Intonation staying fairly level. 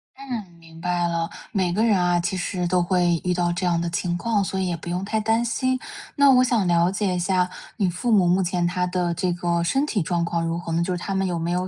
Yes: narrow, 2.3 semitones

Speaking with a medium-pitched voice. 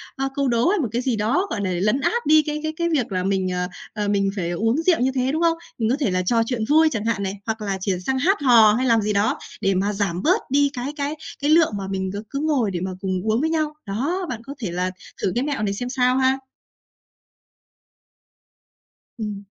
No: high, 235 Hz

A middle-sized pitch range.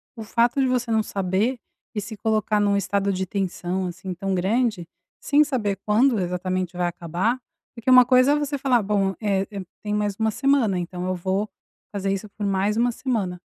Yes: average, 3.9 semitones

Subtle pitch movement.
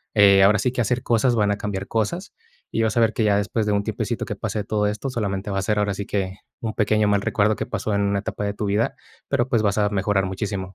Yes: narrow, 1.5 semitones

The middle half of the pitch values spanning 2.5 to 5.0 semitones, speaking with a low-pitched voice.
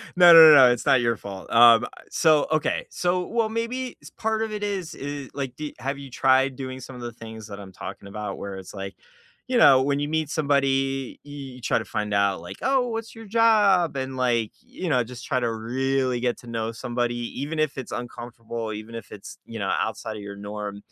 No: wide, 5.5 semitones; low, 130 Hz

